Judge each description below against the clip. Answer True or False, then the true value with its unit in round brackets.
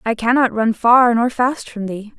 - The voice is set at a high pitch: True (230 Hz)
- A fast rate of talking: True (220 wpm)